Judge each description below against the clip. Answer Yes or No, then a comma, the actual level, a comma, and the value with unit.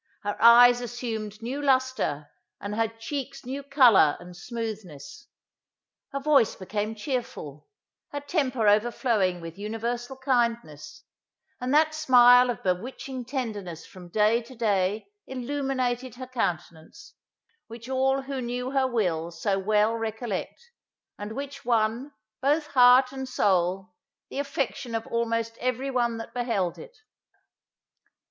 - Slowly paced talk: Yes, slow, 125 wpm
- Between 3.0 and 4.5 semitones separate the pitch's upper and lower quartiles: Yes, average, 3.9 semitones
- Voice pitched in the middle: No, high, 235 Hz